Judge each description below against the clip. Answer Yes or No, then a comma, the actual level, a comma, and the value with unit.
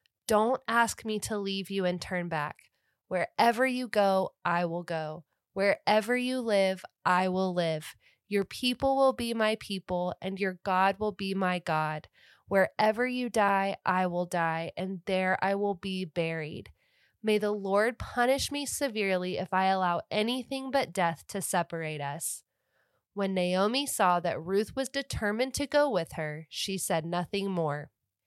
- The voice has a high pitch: Yes, high, 195 Hz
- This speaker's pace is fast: No, average, 160 wpm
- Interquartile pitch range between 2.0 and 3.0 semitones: No, average, 3.5 semitones